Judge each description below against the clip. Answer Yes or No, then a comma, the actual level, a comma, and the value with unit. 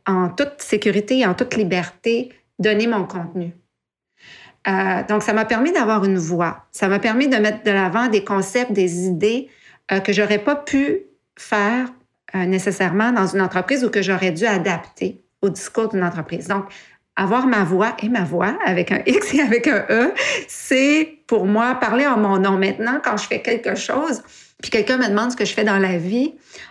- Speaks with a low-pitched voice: No, high, 210 Hz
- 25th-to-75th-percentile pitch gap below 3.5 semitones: No, average, 4.2 semitones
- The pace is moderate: Yes, average, 195 wpm